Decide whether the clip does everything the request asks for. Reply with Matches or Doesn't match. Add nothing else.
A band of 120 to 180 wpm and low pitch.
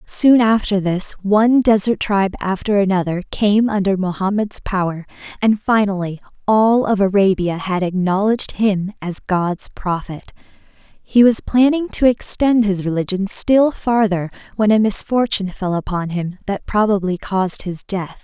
Doesn't match